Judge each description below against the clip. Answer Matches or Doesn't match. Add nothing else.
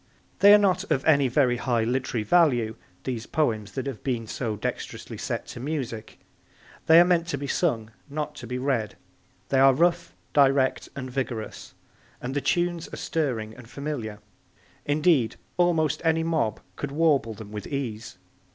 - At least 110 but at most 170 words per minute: Matches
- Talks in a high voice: Doesn't match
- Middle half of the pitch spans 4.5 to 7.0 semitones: Matches